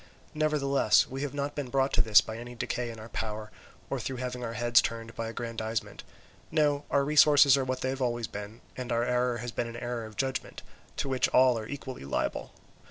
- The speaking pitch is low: Yes, low, 125 Hz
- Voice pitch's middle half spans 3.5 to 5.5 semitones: No, average, 2.8 semitones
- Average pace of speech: No, fast, 215 wpm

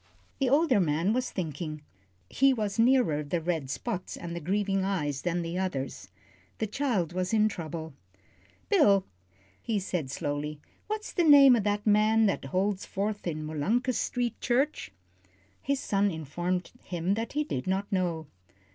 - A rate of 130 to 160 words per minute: Yes, average, 155 wpm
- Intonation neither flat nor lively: No, wide, 5.7 semitones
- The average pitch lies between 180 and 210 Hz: Yes, high, 190 Hz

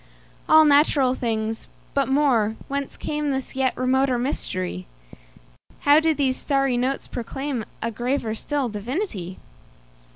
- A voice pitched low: No, very high, 260 Hz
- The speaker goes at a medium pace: No, slow, 100 wpm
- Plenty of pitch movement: No, average, 4.2 semitones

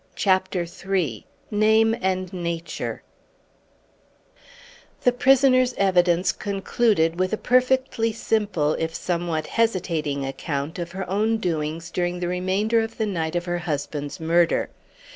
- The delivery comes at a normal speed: No, slow, 125 wpm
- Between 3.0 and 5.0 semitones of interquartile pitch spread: Yes, average, 4.6 semitones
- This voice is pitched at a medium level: Yes, medium, 180 Hz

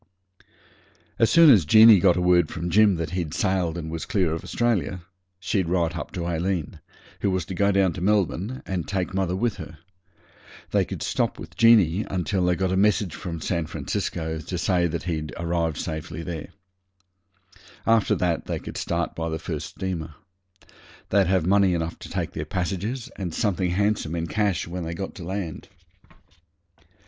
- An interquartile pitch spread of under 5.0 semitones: Yes, average, 2.8 semitones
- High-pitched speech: No, very low, 90 Hz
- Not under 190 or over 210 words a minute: No, average, 175 wpm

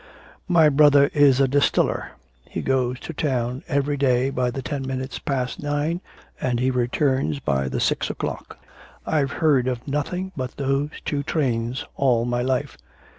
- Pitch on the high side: No, low, 135 Hz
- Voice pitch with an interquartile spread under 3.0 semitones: Yes, narrow, 2.6 semitones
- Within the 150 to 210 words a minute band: Yes, average, 160 wpm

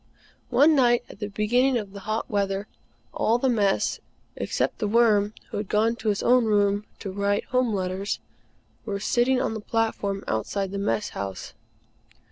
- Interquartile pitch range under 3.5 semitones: Yes, average, 2.8 semitones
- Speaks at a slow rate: No, average, 170 wpm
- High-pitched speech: Yes, high, 210 Hz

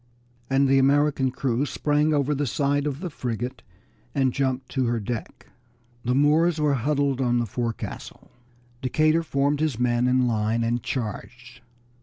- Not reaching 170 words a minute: Yes, average, 155 wpm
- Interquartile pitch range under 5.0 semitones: Yes, average, 3.1 semitones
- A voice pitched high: No, low, 135 Hz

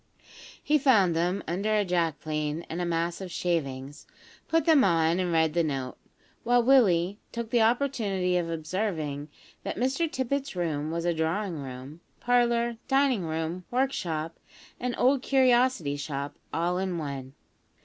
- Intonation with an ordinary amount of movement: No, wide, 6.9 semitones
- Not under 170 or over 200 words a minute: No, average, 150 wpm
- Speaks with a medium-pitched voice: Yes, medium, 175 Hz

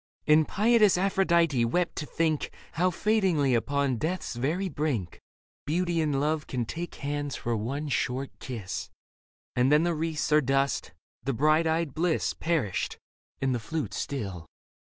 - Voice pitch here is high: No, medium, 150 Hz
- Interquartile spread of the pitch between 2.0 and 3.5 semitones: No, average, 4.2 semitones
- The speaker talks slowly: No, average, 150 wpm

